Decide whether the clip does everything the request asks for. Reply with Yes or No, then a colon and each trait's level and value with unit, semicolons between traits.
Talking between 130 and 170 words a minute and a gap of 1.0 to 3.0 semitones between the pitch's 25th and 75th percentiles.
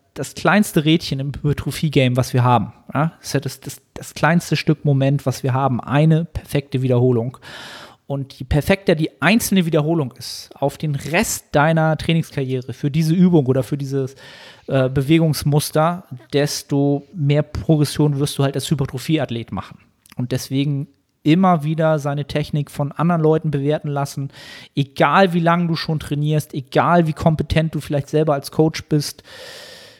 Yes: average, 155 wpm; average, 2.7 semitones